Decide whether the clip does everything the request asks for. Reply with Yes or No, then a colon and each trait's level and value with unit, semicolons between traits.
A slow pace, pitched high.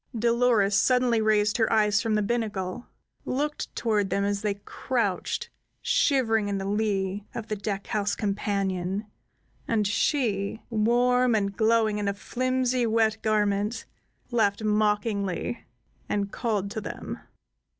Yes: slow, 130 wpm; high, 215 Hz